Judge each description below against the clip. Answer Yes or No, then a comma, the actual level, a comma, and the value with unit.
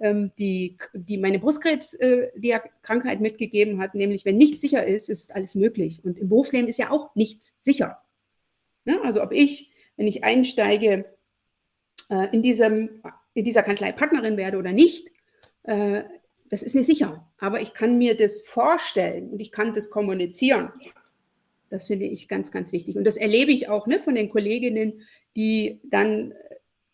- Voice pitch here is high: Yes, high, 220 Hz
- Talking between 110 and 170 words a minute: Yes, average, 155 wpm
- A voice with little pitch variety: No, average, 3.8 semitones